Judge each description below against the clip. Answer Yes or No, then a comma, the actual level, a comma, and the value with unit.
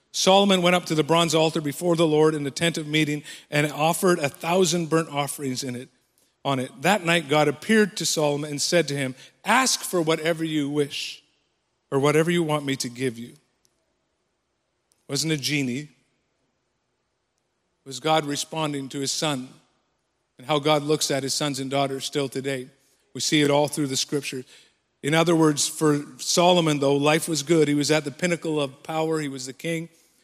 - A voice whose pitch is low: No, medium, 150 Hz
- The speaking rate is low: No, average, 190 wpm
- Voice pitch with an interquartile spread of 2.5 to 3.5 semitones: Yes, average, 2.9 semitones